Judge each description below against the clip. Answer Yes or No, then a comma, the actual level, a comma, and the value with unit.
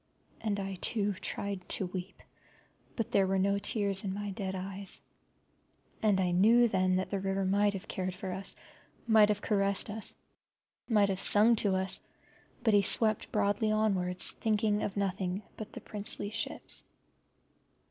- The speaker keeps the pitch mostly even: Yes, narrow, 1.8 semitones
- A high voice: Yes, high, 200 Hz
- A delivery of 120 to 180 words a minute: Yes, average, 160 wpm